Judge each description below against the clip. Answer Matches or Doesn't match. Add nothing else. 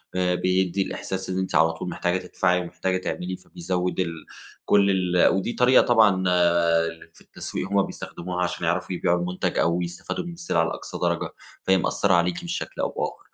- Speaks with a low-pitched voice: Matches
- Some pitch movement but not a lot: Doesn't match